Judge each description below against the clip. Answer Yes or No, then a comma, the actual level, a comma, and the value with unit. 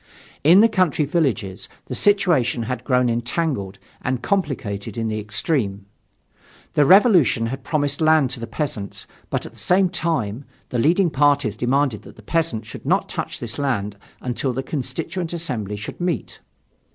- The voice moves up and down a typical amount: No, wide, 6.2 semitones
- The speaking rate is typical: Yes, average, 160 wpm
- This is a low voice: Yes, low, 130 Hz